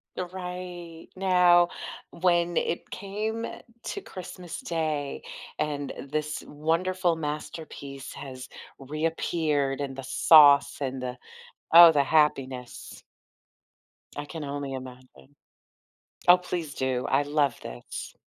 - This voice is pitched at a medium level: Yes, medium, 155 Hz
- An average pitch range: Yes, average, 4.1 semitones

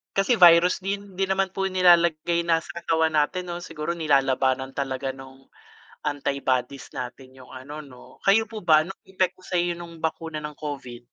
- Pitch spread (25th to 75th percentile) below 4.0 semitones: No, average, 4.8 semitones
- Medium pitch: Yes, medium, 160 Hz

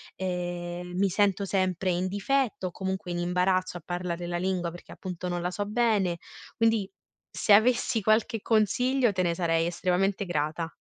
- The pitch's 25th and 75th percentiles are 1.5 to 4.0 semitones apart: Yes, narrow, 2.6 semitones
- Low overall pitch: No, medium, 185 Hz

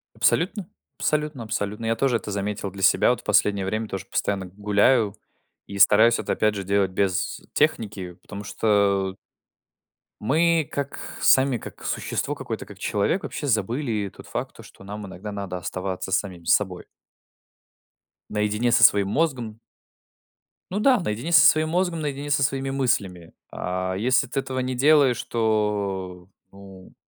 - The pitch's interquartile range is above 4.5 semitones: Yes, average, 5.2 semitones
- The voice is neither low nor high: No, low, 105 Hz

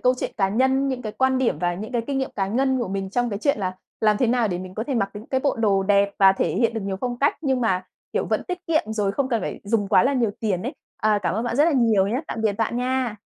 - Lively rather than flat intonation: No, average, 4.6 semitones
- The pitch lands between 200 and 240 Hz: Yes, high, 225 Hz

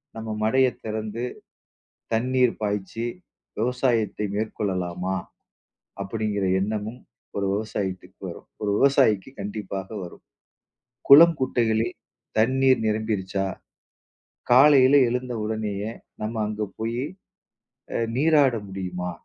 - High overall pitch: No, low, 110 Hz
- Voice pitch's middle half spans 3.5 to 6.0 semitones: Yes, average, 3.9 semitones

